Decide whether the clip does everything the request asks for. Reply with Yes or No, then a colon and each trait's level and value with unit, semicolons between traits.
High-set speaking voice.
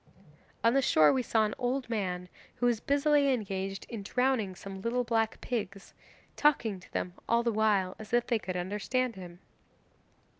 Yes: high, 220 Hz